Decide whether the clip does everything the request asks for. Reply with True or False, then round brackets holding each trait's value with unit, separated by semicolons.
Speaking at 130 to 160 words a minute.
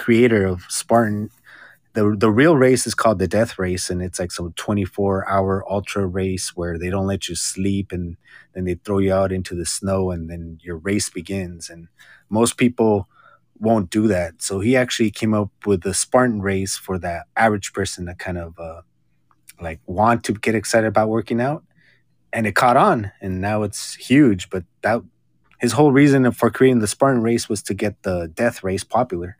False (200 wpm)